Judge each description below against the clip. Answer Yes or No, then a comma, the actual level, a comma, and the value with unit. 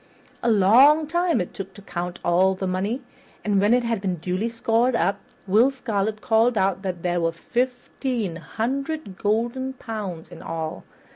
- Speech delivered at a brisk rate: No, average, 165 wpm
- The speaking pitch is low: No, high, 210 Hz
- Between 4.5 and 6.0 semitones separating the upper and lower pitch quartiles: Yes, average, 4.9 semitones